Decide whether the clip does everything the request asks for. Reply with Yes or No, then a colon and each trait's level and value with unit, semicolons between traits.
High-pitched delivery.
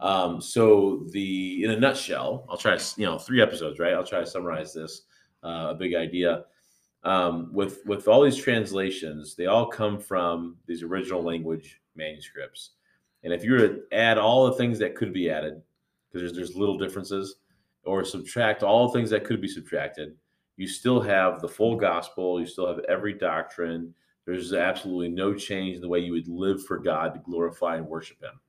No: very low, 95 Hz